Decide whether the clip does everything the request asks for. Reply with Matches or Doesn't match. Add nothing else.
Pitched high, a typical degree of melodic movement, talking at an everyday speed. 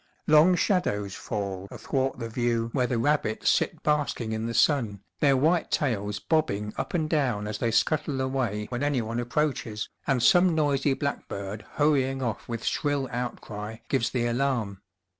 Doesn't match